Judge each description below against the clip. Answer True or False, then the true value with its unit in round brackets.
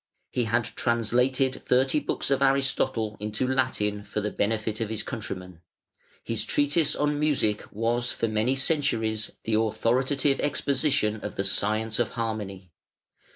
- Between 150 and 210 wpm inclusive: False (140 wpm)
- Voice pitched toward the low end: True (115 Hz)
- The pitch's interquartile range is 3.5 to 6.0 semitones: True (3.8 semitones)